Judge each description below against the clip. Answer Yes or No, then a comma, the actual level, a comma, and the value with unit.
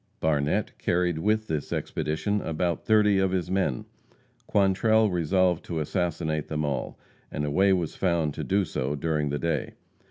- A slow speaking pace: No, average, 160 wpm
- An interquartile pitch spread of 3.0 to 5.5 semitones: Yes, average, 4.0 semitones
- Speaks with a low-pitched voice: Yes, very low, 85 Hz